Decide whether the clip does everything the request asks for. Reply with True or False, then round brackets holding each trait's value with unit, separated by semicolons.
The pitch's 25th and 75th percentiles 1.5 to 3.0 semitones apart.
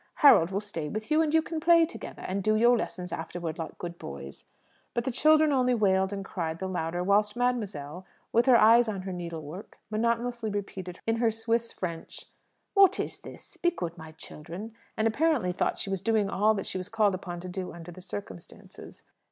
False (4.9 semitones)